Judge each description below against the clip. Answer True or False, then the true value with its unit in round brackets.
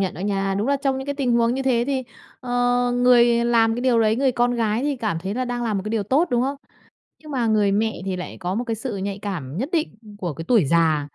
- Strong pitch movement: False (4.3 semitones)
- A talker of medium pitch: False (230 Hz)